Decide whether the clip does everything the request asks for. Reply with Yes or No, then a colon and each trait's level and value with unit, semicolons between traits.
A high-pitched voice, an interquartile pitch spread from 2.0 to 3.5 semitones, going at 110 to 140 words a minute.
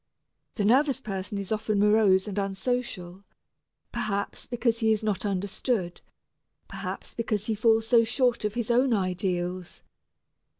Yes: high, 210 Hz; average, 3.0 semitones; slow, 135 wpm